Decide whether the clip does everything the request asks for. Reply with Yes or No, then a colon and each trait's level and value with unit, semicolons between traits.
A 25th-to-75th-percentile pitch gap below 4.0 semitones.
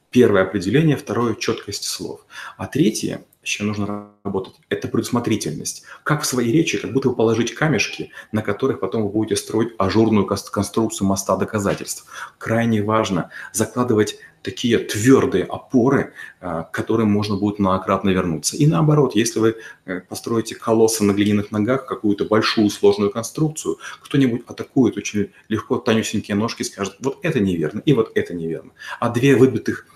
Yes: average, 3.4 semitones